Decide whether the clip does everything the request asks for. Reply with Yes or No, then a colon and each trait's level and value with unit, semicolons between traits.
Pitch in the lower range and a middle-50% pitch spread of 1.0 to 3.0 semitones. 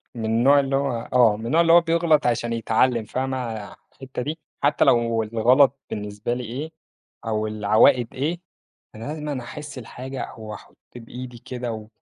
No: low, 125 Hz; average, 3.7 semitones